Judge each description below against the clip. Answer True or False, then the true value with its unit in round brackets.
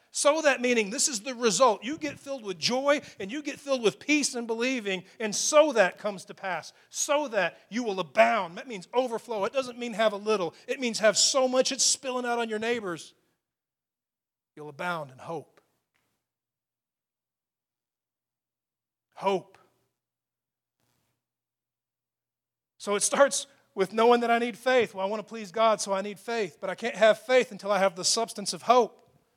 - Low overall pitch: False (225 Hz)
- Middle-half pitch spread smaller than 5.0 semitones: True (4.6 semitones)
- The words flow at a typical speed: True (180 wpm)